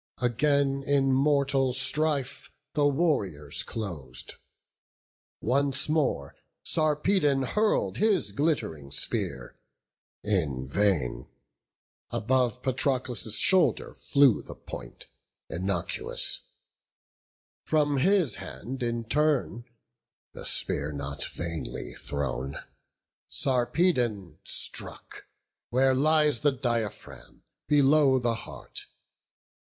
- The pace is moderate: No, slow, 85 wpm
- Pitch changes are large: Yes, wide, 6.8 semitones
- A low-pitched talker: Yes, low, 130 Hz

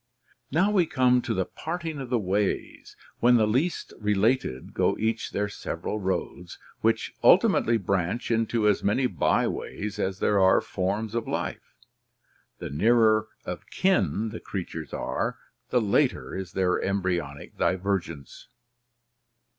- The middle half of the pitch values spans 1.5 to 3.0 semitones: No, average, 4.0 semitones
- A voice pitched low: Yes, low, 105 Hz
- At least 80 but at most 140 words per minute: Yes, slow, 135 wpm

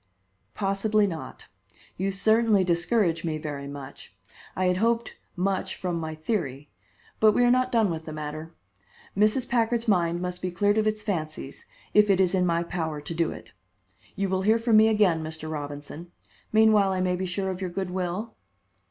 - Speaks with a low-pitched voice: No, medium, 185 Hz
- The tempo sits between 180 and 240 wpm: Yes, average, 185 wpm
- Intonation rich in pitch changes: No, average, 4.5 semitones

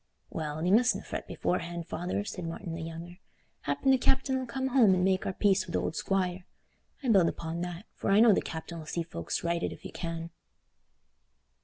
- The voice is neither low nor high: Yes, medium, 180 Hz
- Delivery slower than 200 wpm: No, fast, 205 wpm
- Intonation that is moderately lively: Yes, average, 3.4 semitones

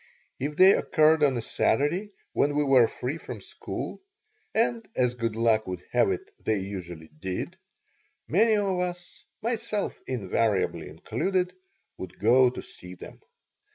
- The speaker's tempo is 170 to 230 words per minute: No, average, 145 wpm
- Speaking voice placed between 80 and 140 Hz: Yes, low, 135 Hz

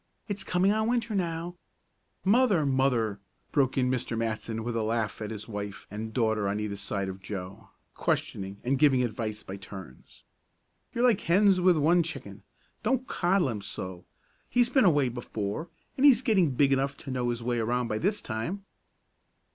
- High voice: No, low, 125 Hz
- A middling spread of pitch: No, wide, 8.8 semitones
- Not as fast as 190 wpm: Yes, average, 180 wpm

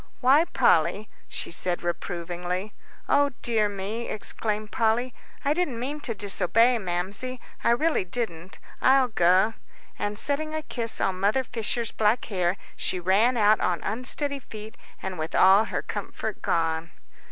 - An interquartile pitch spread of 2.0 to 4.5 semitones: No, average, 5.0 semitones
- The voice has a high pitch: Yes, high, 215 Hz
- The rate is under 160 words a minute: Yes, average, 145 wpm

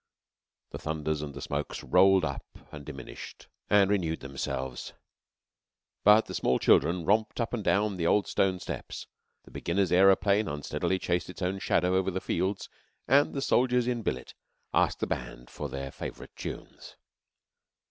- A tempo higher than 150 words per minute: Yes, average, 160 wpm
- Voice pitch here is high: No, very low, 90 Hz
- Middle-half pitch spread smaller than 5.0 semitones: No, wide, 5.5 semitones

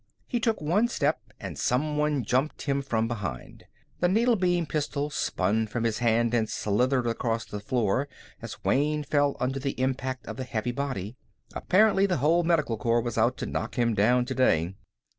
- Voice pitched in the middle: No, low, 130 Hz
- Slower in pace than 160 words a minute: No, average, 180 wpm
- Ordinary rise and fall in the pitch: Yes, average, 4.7 semitones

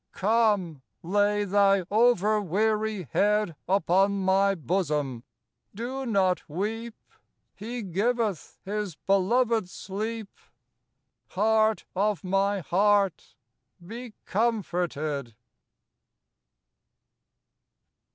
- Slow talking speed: Yes, slow, 75 wpm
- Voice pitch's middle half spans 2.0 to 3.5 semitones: Yes, average, 2.8 semitones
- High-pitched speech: Yes, high, 200 Hz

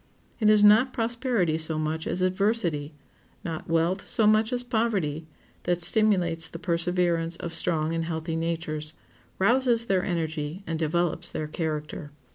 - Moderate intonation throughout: Yes, average, 4.6 semitones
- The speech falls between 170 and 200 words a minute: No, average, 145 wpm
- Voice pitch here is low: No, medium, 170 Hz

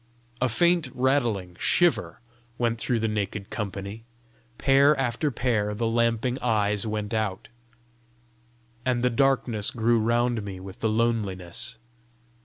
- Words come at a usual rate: No, slow, 125 wpm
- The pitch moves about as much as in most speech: Yes, average, 3.0 semitones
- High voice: No, low, 115 Hz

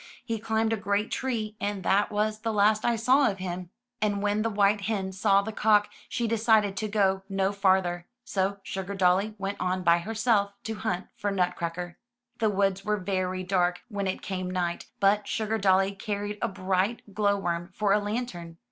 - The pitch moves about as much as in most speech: No, narrow, 2.3 semitones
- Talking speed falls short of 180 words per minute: No, average, 185 wpm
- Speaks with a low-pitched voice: No, high, 200 Hz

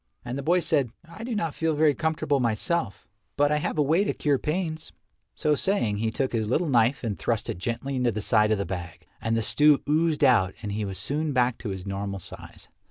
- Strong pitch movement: Yes, wide, 6.4 semitones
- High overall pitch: No, low, 130 Hz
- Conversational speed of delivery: No, fast, 230 wpm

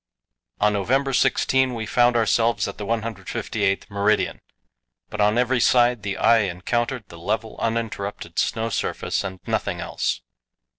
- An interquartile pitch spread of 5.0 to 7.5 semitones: No, average, 2.8 semitones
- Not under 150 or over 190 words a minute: No, average, 140 wpm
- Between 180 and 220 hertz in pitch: No, low, 110 Hz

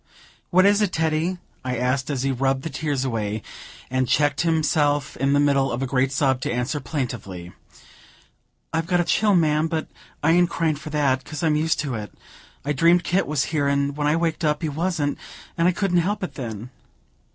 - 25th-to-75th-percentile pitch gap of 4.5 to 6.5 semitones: No, average, 3.7 semitones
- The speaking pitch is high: No, medium, 145 Hz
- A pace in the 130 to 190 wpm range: No, fast, 205 wpm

